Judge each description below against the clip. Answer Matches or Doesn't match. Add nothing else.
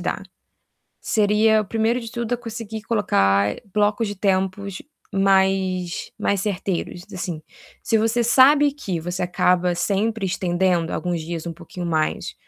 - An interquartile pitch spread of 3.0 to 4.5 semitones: Matches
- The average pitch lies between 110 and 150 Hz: Doesn't match